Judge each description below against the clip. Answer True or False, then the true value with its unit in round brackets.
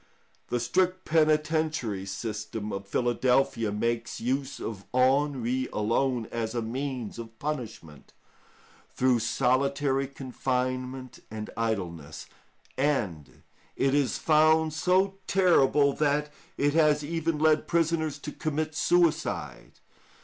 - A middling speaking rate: False (105 wpm)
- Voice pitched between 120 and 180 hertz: True (135 Hz)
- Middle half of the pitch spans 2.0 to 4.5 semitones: False (5.0 semitones)